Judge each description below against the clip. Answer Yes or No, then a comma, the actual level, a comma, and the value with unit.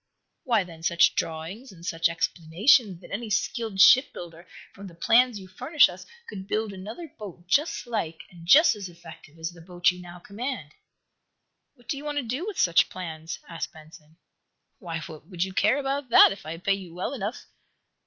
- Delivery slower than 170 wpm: No, average, 185 wpm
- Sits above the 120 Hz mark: Yes, high, 190 Hz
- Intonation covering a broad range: Yes, wide, 5.9 semitones